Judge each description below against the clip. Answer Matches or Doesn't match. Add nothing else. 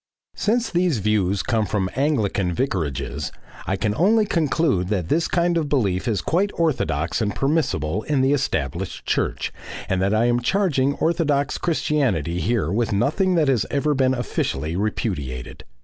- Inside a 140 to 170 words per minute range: Matches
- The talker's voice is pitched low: Matches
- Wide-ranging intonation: Matches